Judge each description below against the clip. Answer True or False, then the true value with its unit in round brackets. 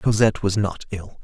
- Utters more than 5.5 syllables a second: False (5.2 syllables/s)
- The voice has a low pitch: True (100 Hz)